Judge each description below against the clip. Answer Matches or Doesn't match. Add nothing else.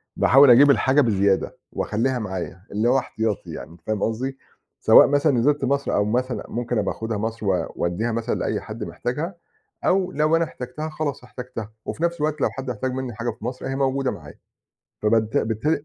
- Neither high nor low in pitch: Doesn't match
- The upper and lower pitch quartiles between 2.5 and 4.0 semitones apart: Doesn't match